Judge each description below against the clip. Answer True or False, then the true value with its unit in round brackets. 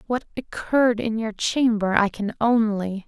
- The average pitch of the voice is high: True (220 Hz)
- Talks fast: False (155 wpm)